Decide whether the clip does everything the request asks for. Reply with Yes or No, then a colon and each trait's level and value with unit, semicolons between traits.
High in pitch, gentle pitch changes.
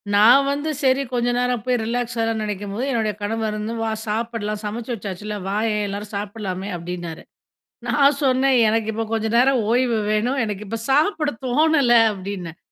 No: high, 225 Hz; average, 3.2 semitones